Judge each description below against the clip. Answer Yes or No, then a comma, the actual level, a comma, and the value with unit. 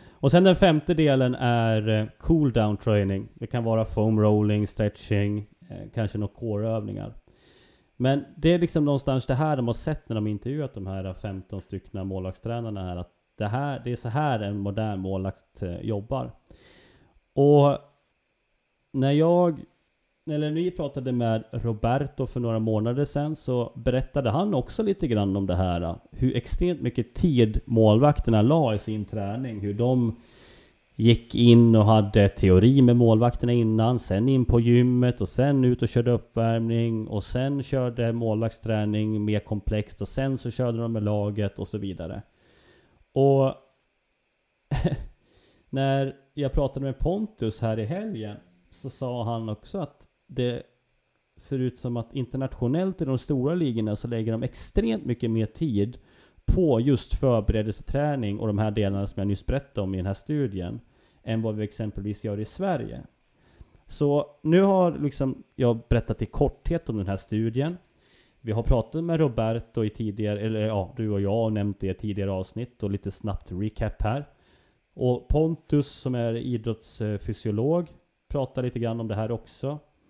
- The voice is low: Yes, low, 115 Hz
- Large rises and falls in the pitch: No, average, 4.2 semitones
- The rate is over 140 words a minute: Yes, average, 165 wpm